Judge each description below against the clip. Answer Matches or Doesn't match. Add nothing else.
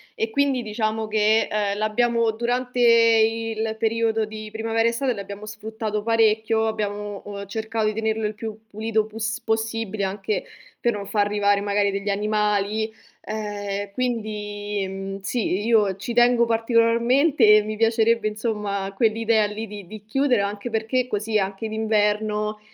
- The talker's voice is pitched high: Matches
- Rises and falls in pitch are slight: Matches